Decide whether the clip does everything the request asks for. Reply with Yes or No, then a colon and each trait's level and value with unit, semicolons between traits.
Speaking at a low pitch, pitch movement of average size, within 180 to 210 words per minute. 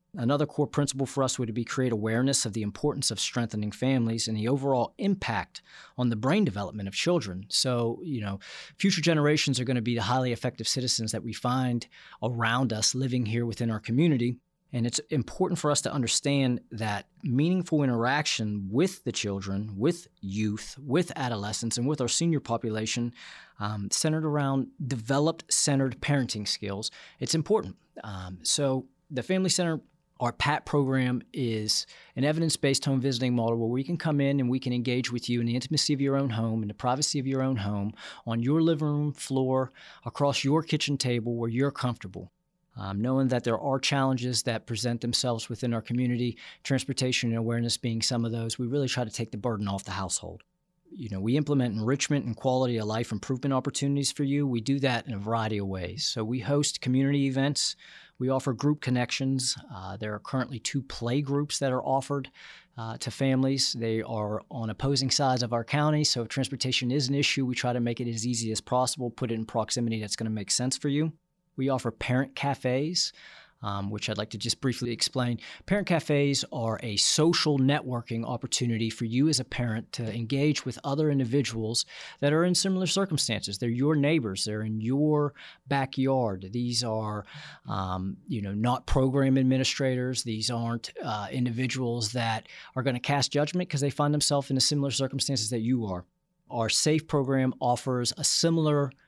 Yes: low, 125 Hz; average, 3.6 semitones; average, 190 wpm